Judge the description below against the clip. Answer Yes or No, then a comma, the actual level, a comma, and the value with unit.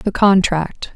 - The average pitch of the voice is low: No, medium, 185 Hz